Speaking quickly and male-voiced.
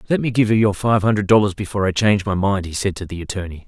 Yes: fast, 295 wpm; male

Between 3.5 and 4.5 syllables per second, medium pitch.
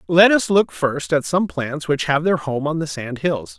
Yes: 4.4 syllables/s; medium, 155 Hz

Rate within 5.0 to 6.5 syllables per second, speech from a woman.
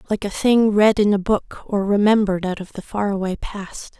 Yes: 5.2 syllables/s; female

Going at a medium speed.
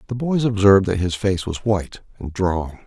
No: fast, 210 wpm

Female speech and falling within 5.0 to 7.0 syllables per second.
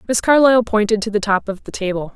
Yes: female; 6.5 syllables/s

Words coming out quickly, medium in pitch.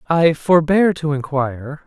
No: slow, 130 wpm; medium, 155 Hz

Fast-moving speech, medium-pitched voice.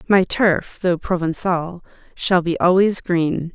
No: slow, 135 wpm; medium, 180 Hz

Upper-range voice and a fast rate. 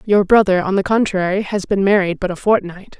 Yes: high, 195 Hz; fast, 220 wpm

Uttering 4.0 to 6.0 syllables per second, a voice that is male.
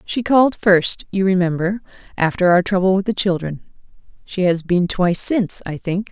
No: 5.2 syllables/s; female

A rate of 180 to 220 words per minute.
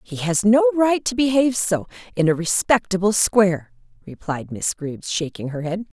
No: average, 170 wpm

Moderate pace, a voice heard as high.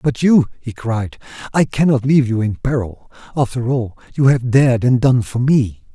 No: average, 190 wpm; low, 125 Hz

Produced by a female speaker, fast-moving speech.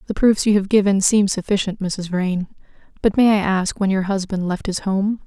Yes: female; fast, 215 wpm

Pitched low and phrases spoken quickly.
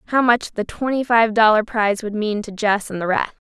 No: high, 220 Hz; fast, 240 wpm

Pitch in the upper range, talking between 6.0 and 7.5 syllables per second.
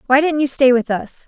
No: very high, 265 Hz; 5.4 syllables/s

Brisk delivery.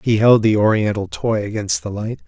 Yes: fast, 210 wpm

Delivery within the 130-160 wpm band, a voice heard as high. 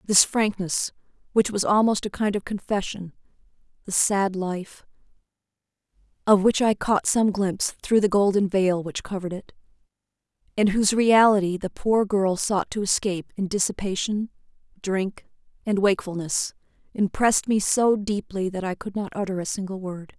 Yes: average, 150 wpm; high, 195 Hz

